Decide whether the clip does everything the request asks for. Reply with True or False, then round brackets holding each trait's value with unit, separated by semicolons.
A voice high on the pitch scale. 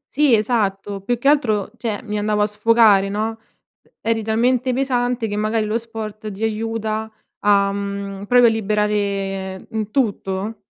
True (215 Hz)